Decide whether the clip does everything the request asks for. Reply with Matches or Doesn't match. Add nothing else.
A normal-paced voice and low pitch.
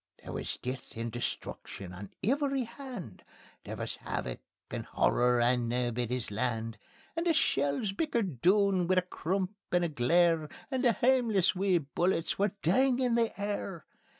Doesn't match